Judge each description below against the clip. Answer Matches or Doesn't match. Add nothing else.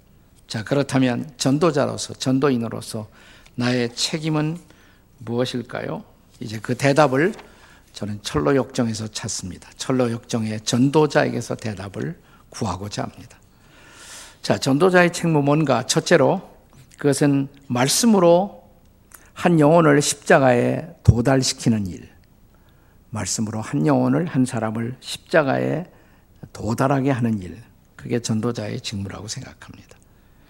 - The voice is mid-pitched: Doesn't match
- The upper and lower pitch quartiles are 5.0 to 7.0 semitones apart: Doesn't match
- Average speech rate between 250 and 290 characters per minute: Matches